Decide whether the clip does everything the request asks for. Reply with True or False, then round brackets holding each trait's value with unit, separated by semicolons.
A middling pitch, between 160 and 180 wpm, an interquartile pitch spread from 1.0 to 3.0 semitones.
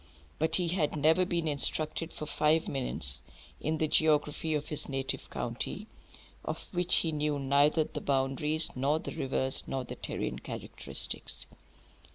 False (150 Hz; 150 wpm; 2.6 semitones)